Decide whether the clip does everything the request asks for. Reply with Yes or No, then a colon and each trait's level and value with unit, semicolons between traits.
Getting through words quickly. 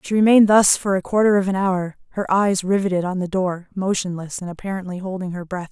Yes: fast, 220 wpm